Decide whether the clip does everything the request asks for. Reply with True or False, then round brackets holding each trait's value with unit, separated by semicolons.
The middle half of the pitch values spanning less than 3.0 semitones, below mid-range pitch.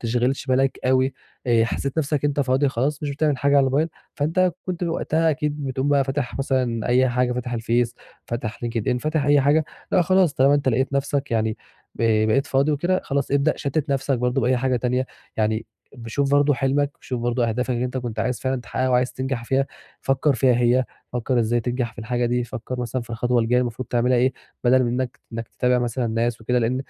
True (2.5 semitones; 130 Hz)